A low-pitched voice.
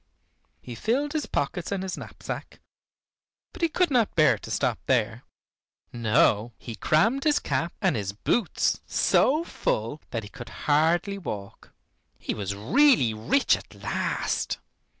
No: medium, 155 Hz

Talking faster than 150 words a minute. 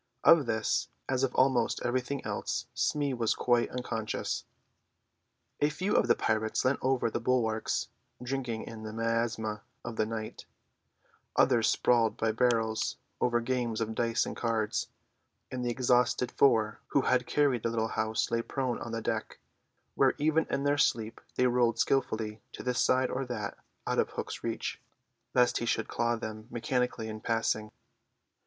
Yes: average, 160 wpm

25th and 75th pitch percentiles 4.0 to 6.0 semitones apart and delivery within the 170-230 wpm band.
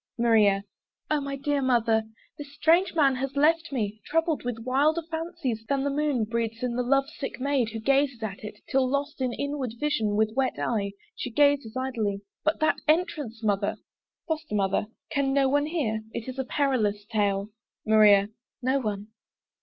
Yes: average, 4.7 semitones; average, 175 wpm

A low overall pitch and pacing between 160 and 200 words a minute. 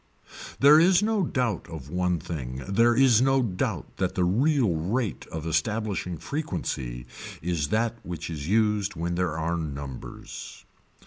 No: very low, 90 Hz; average, 145 wpm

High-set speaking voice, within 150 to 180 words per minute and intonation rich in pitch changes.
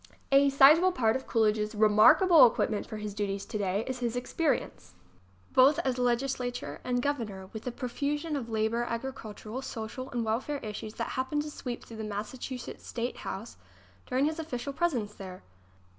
No: high, 245 Hz; average, 165 wpm; average, 4.0 semitones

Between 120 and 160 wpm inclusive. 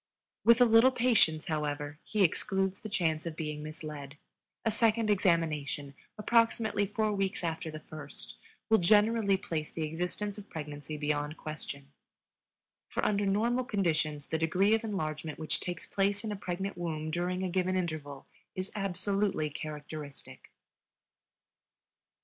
Yes: average, 140 wpm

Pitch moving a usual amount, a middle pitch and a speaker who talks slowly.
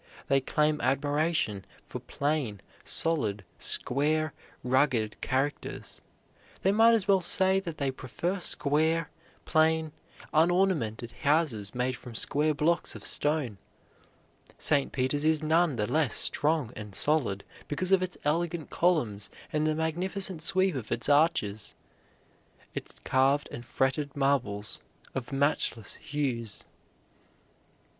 Yes: average, 4.2 semitones; medium, 145 Hz; slow, 120 wpm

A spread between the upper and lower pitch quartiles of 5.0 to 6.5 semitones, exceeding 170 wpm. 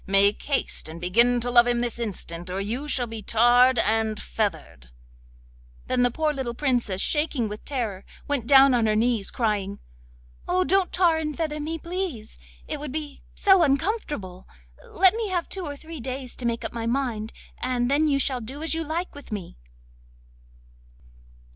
Yes: wide, 5.4 semitones; average, 180 wpm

